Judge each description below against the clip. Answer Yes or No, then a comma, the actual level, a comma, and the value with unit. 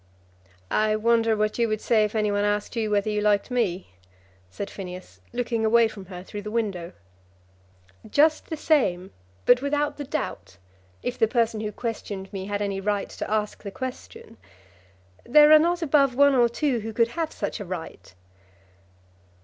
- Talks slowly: No, average, 175 wpm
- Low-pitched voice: No, high, 220 Hz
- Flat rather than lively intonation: No, average, 3.6 semitones